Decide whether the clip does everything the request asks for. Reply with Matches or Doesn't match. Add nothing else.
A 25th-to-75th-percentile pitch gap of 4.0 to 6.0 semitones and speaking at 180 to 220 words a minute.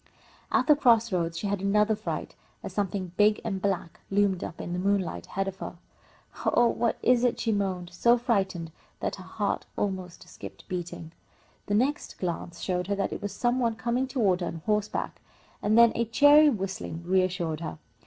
Matches